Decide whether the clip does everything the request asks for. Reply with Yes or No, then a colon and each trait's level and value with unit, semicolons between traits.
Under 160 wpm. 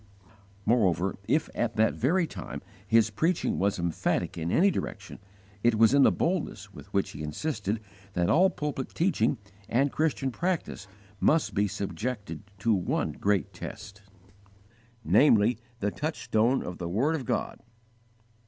Yes: average, 145 wpm